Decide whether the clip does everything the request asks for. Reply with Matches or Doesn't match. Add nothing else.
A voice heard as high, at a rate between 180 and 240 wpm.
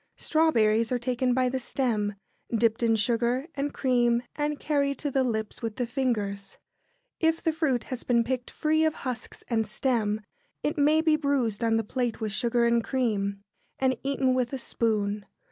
Matches